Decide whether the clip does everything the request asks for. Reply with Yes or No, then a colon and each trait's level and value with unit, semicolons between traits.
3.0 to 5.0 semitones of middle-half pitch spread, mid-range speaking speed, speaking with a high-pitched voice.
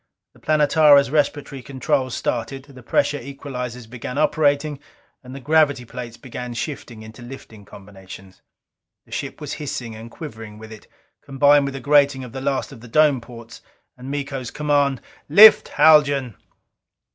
No: average, 3.3 semitones; average, 150 wpm; low, 135 Hz